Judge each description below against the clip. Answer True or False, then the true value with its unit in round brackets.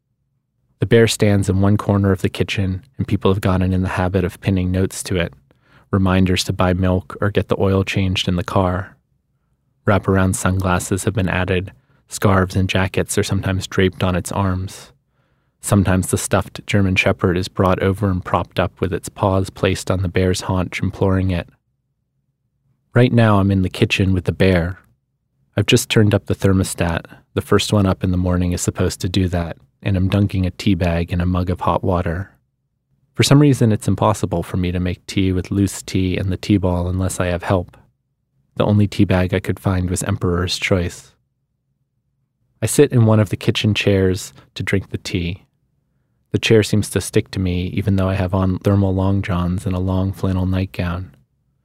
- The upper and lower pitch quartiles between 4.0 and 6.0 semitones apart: False (3.1 semitones)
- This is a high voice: False (100 Hz)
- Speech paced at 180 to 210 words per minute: True (200 wpm)